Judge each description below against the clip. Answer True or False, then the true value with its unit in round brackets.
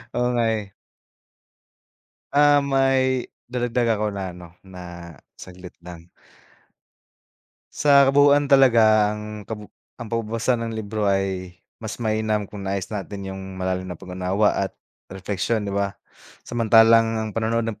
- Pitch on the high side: False (110 Hz)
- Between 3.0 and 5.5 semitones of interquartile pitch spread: True (3.3 semitones)